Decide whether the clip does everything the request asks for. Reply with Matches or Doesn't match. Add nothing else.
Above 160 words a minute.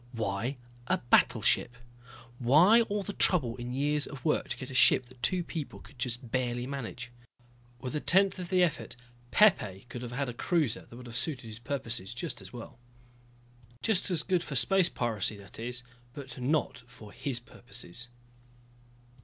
Matches